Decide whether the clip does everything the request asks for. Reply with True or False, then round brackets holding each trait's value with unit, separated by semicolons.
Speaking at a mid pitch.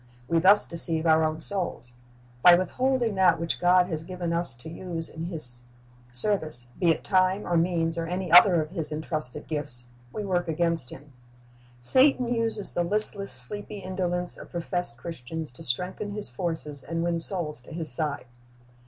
True (170 Hz)